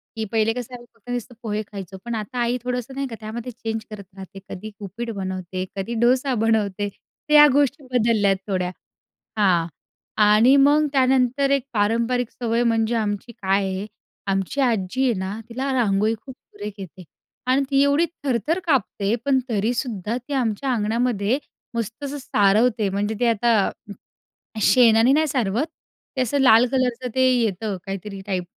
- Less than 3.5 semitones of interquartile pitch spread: No, average, 3.8 semitones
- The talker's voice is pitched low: No, high, 230 Hz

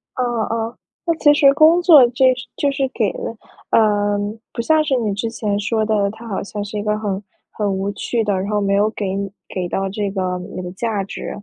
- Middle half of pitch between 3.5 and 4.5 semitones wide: No, average, 3.0 semitones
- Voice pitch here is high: Yes, high, 210 Hz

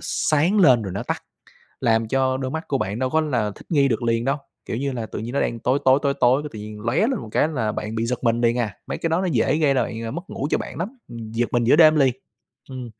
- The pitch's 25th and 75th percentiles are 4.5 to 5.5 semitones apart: No, average, 4.1 semitones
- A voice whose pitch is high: No, low, 125 Hz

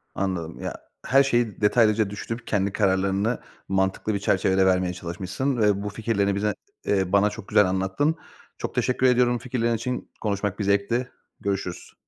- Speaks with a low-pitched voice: Yes, low, 100 Hz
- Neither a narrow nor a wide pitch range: Yes, average, 3.3 semitones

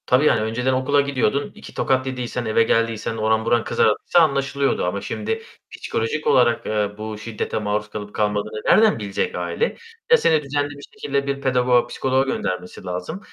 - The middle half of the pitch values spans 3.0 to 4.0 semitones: No, average, 4.5 semitones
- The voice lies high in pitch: No, low, 120 Hz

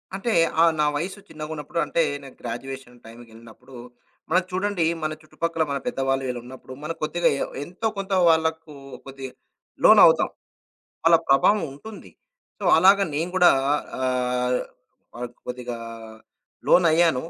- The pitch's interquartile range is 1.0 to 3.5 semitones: No, average, 5.0 semitones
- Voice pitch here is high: No, medium, 150 Hz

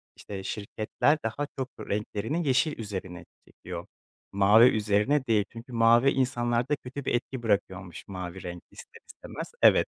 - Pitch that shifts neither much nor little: Yes, average, 4.5 semitones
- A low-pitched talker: Yes, low, 115 Hz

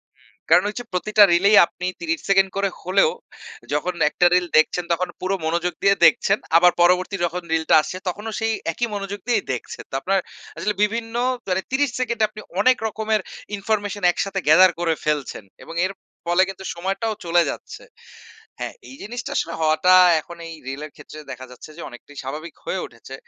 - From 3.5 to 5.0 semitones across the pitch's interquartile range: Yes, average, 3.8 semitones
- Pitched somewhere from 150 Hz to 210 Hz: Yes, medium, 185 Hz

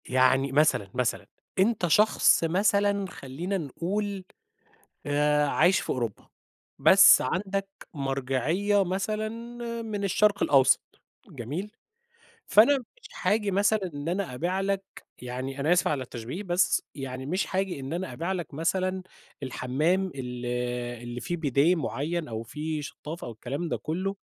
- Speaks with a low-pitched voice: No, medium, 165 Hz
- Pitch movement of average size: No, wide, 6.3 semitones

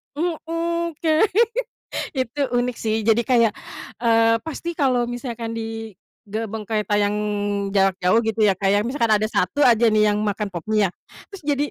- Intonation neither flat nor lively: Yes, average, 3.9 semitones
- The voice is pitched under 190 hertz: No, high, 230 Hz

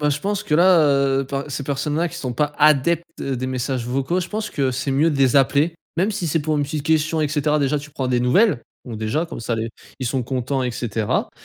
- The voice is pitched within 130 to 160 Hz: Yes, medium, 140 Hz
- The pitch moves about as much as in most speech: Yes, average, 3.3 semitones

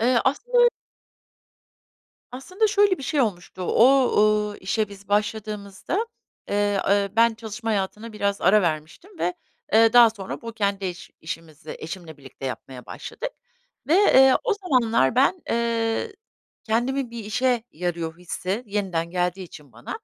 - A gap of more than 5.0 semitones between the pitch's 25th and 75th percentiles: Yes, wide, 5.4 semitones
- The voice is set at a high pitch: Yes, high, 215 Hz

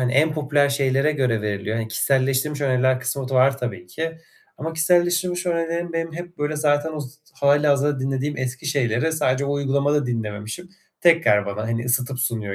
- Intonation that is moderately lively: Yes, average, 3.7 semitones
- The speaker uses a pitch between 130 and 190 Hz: Yes, medium, 140 Hz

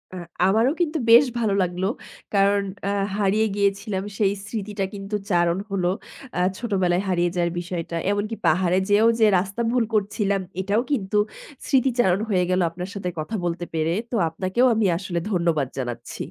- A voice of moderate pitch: No, high, 195 Hz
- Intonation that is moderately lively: Yes, average, 3.2 semitones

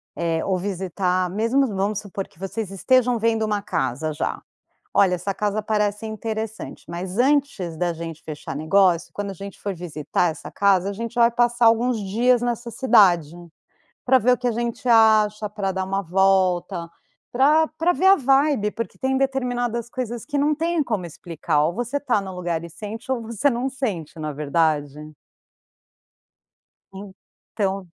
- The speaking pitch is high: Yes, high, 205 Hz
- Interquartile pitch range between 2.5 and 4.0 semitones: No, average, 4.9 semitones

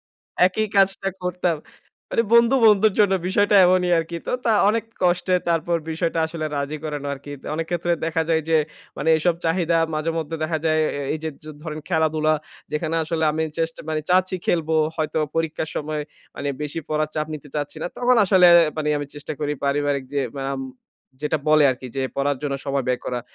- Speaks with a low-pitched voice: No, medium, 160 Hz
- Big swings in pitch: No, average, 2.7 semitones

